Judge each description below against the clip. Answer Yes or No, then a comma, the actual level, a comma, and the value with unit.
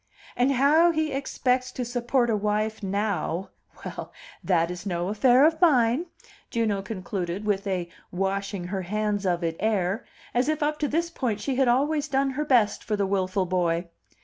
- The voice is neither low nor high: No, high, 215 Hz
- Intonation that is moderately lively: No, wide, 5.8 semitones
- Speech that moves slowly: No, average, 175 wpm